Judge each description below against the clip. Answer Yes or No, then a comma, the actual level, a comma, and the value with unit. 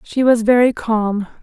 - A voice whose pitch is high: Yes, high, 225 Hz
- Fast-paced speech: No, average, 170 wpm